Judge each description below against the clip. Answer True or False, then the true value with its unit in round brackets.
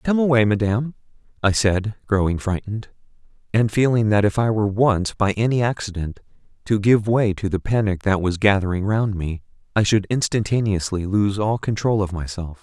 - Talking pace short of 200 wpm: True (170 wpm)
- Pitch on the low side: True (105 Hz)